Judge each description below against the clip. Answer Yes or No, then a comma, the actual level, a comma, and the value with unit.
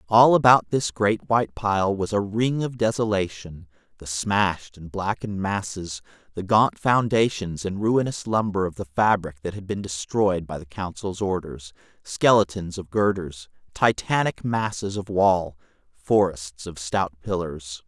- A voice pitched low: Yes, low, 100 Hz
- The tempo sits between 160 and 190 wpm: No, average, 150 wpm